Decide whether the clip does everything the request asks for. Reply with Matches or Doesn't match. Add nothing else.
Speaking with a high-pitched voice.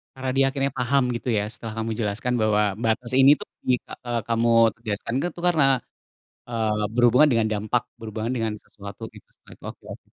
Doesn't match